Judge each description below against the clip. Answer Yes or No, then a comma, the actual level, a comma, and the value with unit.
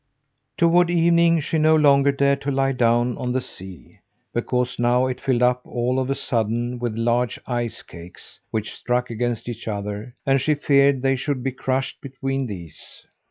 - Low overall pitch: Yes, low, 125 Hz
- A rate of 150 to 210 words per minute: Yes, average, 175 wpm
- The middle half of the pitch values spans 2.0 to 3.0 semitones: Yes, narrow, 2.5 semitones